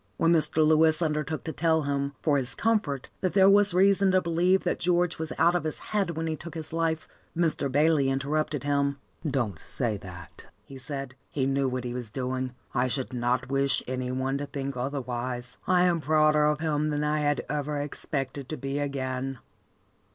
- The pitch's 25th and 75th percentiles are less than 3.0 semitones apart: No, average, 3.3 semitones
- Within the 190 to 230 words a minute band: Yes, average, 195 wpm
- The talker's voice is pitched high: No, medium, 145 Hz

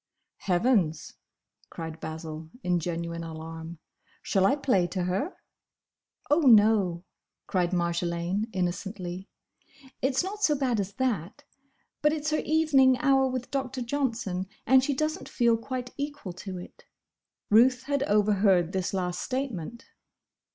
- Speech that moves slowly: Yes, slow, 130 wpm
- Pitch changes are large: Yes, wide, 7.0 semitones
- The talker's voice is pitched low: No, high, 205 Hz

